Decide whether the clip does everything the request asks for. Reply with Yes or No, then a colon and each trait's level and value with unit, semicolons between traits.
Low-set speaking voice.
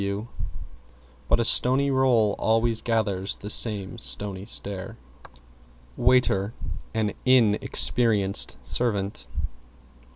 Yes: low, 110 Hz